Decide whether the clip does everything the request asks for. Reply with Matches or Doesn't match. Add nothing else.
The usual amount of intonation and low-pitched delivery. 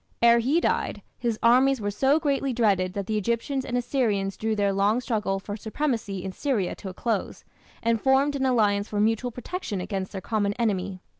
Doesn't match